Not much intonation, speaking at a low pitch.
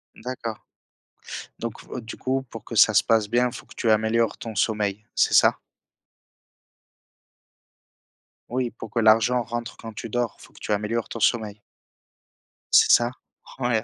Yes: narrow, 1.8 semitones; low, 115 Hz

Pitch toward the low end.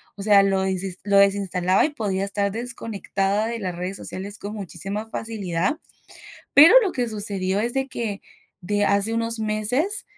No: high, 205 Hz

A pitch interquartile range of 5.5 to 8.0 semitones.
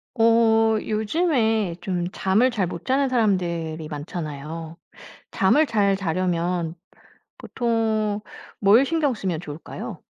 No: average, 5.1 semitones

